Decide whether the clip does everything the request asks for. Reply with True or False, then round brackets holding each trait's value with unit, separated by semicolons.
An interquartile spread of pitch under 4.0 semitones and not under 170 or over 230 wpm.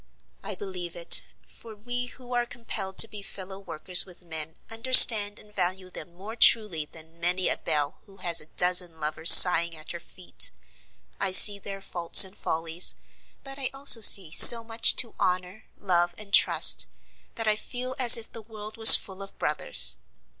False (4.5 semitones; 180 wpm)